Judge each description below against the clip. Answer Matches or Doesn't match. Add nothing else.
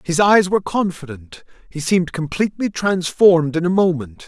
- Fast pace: Doesn't match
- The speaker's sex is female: Doesn't match